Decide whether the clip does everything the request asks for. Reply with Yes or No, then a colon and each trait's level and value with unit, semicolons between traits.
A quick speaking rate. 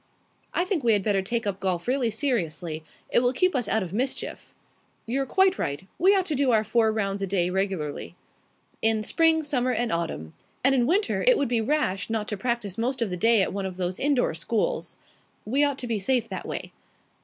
Yes: fast, 215 wpm